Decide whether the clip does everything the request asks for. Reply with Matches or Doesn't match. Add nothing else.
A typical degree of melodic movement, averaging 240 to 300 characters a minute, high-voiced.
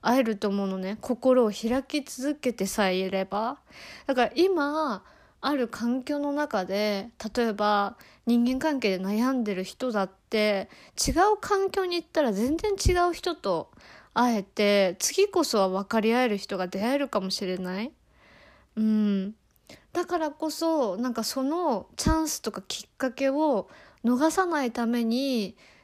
Doesn't match